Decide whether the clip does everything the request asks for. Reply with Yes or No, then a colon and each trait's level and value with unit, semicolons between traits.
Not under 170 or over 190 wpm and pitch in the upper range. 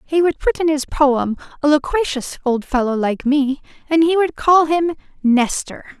Yes: average, 180 wpm; very high, 290 Hz